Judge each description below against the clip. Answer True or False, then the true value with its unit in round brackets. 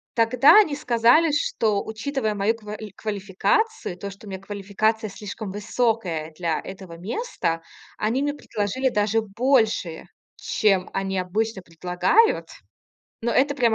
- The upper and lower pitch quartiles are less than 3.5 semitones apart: False (4.1 semitones)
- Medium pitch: False (215 Hz)